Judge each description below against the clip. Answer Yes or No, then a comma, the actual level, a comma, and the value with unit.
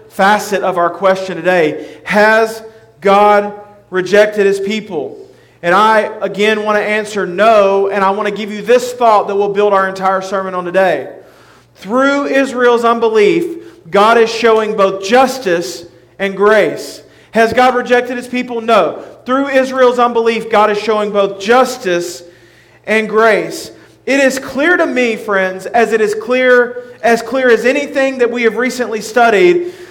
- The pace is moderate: Yes, average, 155 wpm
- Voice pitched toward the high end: Yes, high, 220 Hz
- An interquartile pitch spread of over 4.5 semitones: No, average, 4.0 semitones